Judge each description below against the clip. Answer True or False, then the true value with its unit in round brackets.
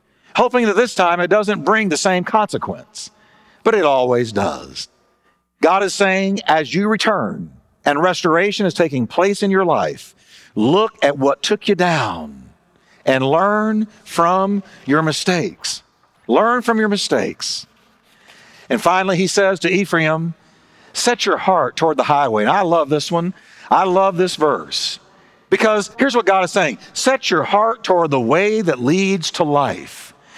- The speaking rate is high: False (160 wpm)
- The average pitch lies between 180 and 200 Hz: True (190 Hz)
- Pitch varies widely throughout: False (4.4 semitones)